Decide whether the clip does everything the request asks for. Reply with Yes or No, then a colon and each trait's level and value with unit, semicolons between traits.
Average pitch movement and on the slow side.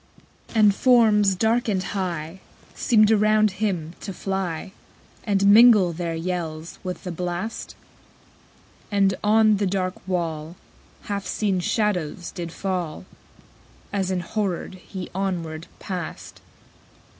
Yes: average, 3.3 semitones; slow, 120 wpm